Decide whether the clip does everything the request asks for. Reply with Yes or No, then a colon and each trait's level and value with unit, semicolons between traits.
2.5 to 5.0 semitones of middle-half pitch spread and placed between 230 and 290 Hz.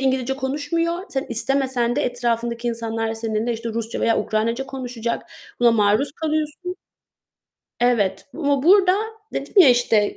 Yes: average, 3.6 semitones; high, 245 Hz